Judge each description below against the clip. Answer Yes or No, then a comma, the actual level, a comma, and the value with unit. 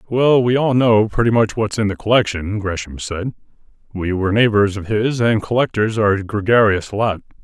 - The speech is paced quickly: No, average, 185 wpm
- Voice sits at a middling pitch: No, low, 105 Hz